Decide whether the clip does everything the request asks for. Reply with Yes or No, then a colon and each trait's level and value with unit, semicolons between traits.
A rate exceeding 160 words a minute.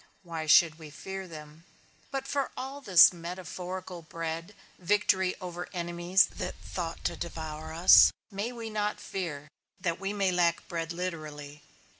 No: average, 145 wpm